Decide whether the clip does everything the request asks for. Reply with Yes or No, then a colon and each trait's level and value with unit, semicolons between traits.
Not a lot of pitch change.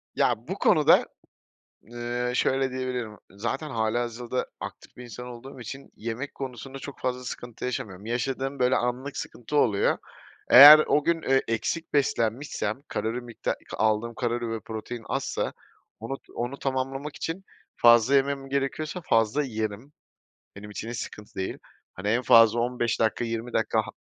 No: average, 3.0 semitones